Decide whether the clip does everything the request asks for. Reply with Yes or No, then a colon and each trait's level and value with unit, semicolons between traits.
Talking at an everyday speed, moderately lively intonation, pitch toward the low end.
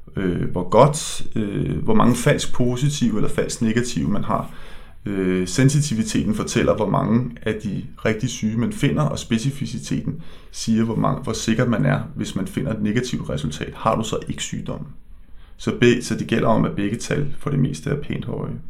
No: average, 190 wpm; wide, 7.6 semitones; low, 110 Hz